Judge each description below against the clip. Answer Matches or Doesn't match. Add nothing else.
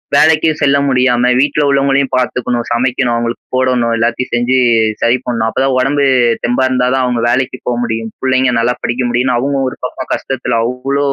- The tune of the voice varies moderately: Doesn't match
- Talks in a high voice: Doesn't match